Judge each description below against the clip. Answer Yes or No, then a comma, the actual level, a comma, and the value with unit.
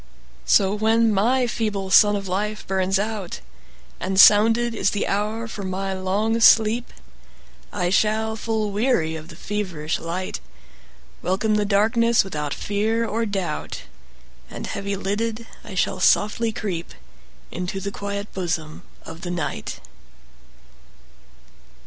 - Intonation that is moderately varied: Yes, average, 3.0 semitones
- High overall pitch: Yes, high, 200 Hz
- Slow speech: Yes, slow, 115 wpm